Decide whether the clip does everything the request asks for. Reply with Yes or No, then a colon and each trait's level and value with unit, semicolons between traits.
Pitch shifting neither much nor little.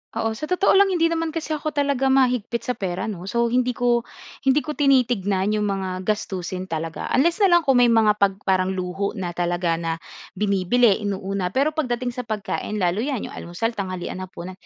No: wide, 5.8 semitones